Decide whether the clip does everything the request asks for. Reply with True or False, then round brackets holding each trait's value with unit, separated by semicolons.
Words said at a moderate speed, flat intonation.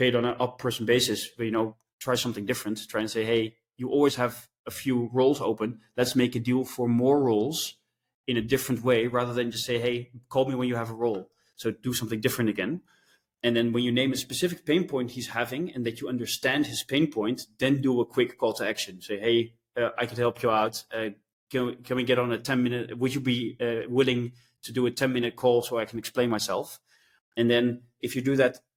False (230 wpm; 1.6 semitones)